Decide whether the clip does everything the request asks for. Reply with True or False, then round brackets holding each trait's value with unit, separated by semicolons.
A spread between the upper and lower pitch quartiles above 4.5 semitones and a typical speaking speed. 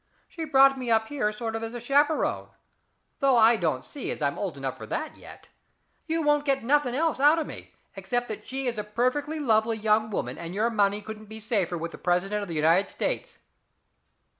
False (4.9 semitones; 215 wpm)